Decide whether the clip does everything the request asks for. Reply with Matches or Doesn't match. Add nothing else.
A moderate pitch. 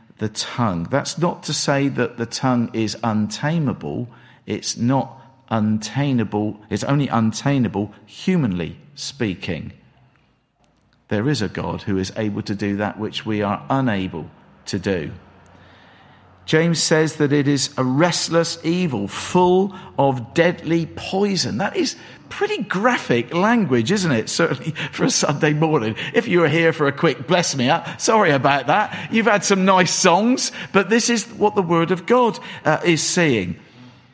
Matches